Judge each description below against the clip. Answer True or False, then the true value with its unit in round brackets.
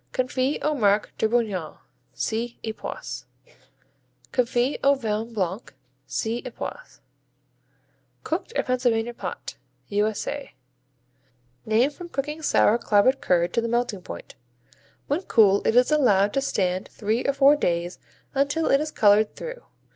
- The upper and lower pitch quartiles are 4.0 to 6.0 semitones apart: True (4.8 semitones)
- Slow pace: True (130 wpm)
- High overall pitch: True (235 Hz)